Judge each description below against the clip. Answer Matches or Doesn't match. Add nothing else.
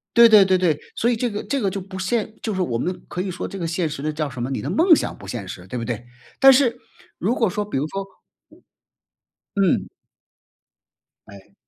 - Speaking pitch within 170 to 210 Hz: Matches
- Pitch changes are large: Matches